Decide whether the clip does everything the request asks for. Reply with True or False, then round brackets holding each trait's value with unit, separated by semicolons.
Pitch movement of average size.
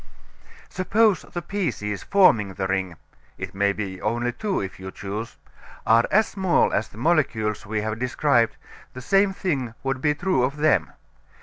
False (8.7 semitones)